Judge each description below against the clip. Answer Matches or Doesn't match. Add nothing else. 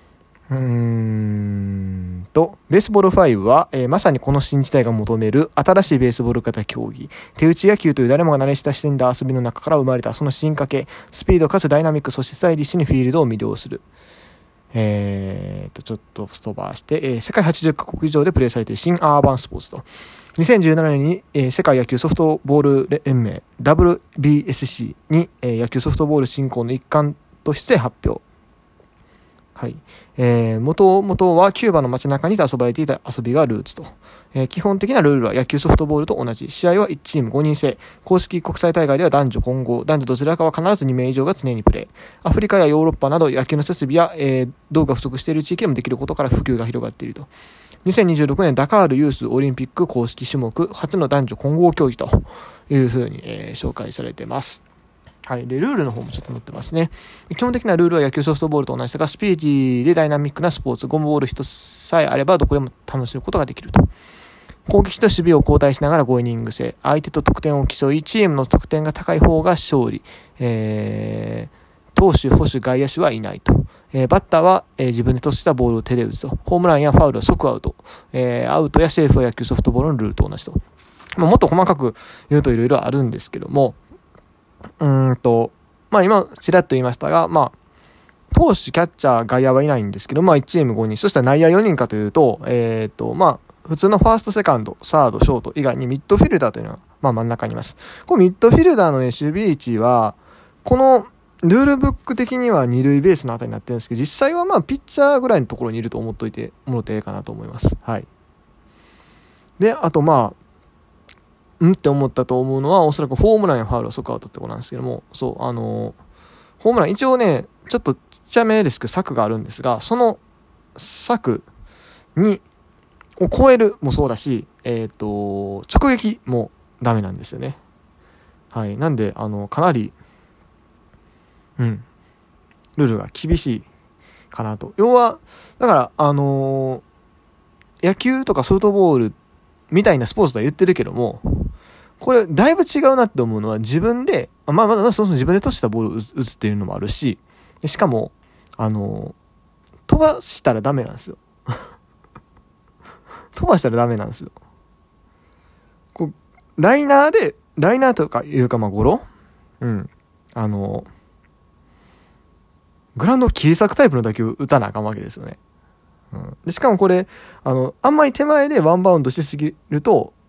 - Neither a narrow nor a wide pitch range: Doesn't match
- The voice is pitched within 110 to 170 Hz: Matches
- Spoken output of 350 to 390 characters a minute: Matches